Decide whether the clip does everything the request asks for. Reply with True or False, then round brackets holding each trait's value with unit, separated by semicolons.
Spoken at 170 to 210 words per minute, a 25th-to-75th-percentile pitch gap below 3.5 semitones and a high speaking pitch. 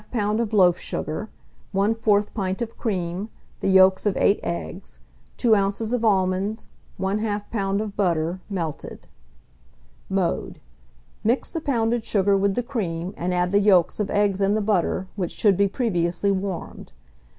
False (150 wpm; 2.6 semitones; 200 Hz)